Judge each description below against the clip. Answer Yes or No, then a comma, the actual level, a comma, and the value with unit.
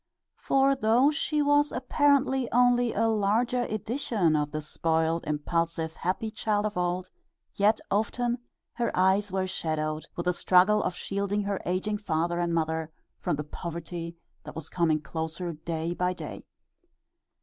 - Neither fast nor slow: Yes, average, 150 wpm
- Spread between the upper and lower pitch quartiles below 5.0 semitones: No, average, 5.3 semitones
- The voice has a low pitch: No, medium, 185 Hz